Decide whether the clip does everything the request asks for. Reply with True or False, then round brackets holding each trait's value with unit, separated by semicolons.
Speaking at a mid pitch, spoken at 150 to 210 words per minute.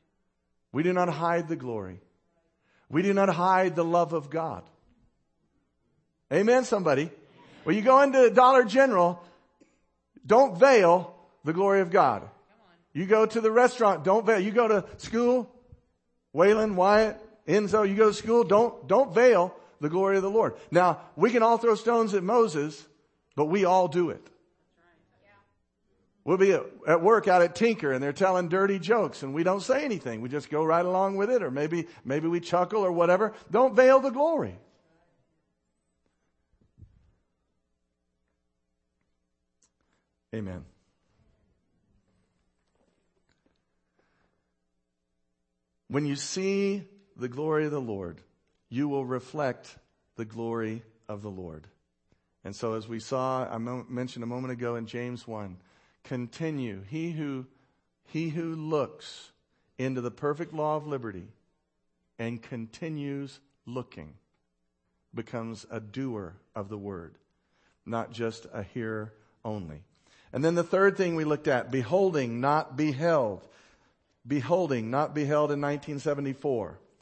False (145 Hz; 135 wpm)